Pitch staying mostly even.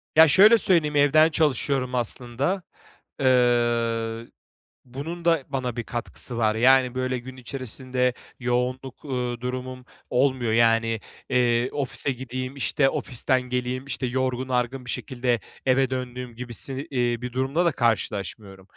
Yes: narrow, 1.8 semitones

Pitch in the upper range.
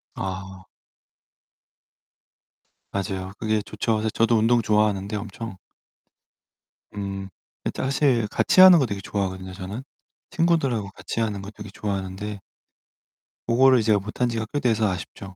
No: low, 105 Hz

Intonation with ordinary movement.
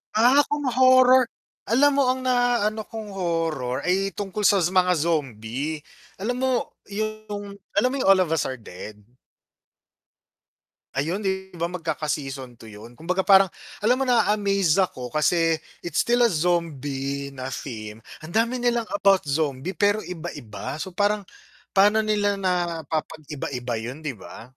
No: wide, 6.6 semitones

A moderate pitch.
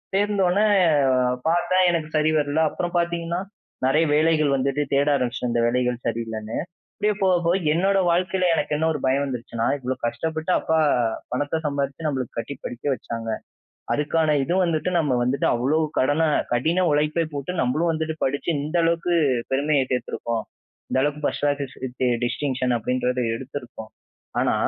Yes: medium, 145 Hz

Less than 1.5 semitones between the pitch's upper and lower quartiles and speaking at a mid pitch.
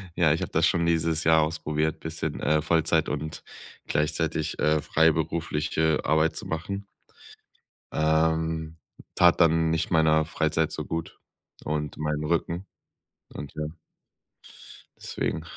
No: narrow, 1.0 semitones; very low, 80 Hz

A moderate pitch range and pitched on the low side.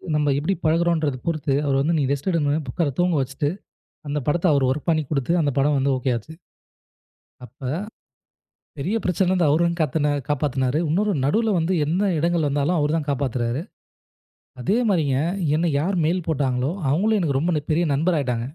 No: average, 3.5 semitones; medium, 150 Hz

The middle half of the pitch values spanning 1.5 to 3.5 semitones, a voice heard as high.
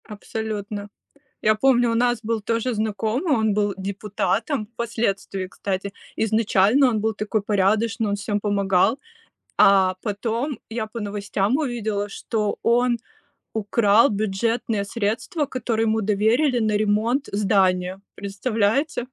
Yes: narrow, 2.5 semitones; high, 215 Hz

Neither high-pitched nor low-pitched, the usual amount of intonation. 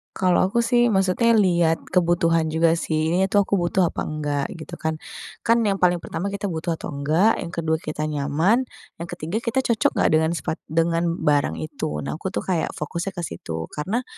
Yes: medium, 170 Hz; average, 3.6 semitones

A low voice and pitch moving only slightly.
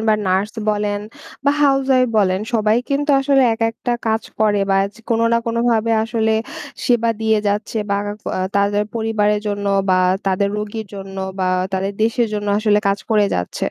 No: high, 215 Hz; narrow, 2.1 semitones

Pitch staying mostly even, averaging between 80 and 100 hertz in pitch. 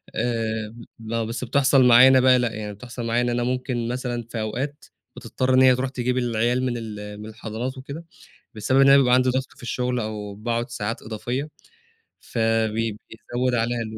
No: narrow, 2.3 semitones; low, 120 Hz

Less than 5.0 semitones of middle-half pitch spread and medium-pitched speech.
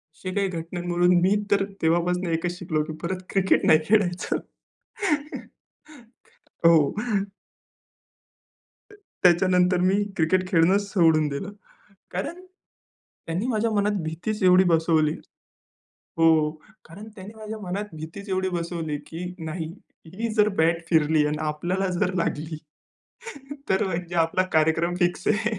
Yes: average, 2.9 semitones; medium, 180 Hz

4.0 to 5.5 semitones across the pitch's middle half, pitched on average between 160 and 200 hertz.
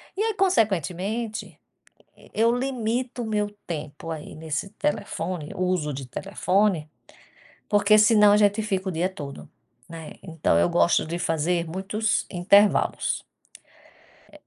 Yes: average, 4.7 semitones; high, 190 Hz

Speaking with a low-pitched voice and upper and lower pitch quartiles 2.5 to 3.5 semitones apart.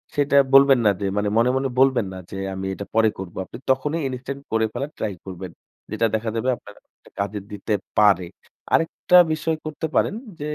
No: low, 115 Hz; average, 5.2 semitones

